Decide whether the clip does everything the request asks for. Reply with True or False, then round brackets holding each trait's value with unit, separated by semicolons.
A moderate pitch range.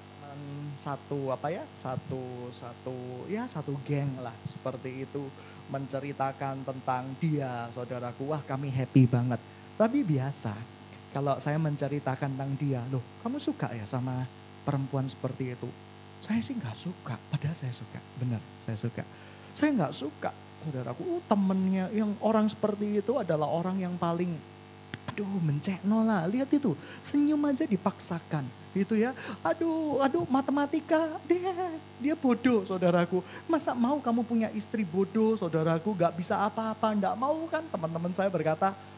False (8.9 semitones)